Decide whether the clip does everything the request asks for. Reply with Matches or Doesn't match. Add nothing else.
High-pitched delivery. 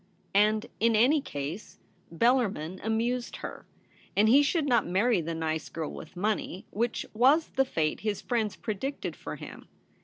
Matches